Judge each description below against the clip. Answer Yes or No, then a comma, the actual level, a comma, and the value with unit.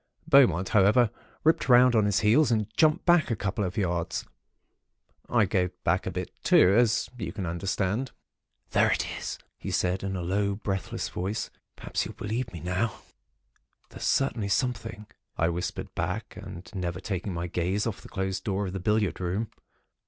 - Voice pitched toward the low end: Yes, low, 100 Hz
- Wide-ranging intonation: No, average, 3.5 semitones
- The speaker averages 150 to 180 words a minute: Yes, average, 170 wpm